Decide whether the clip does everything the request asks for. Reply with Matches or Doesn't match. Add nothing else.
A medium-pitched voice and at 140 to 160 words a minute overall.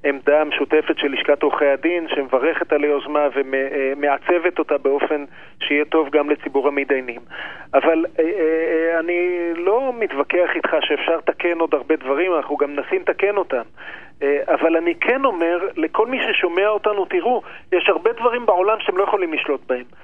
Matches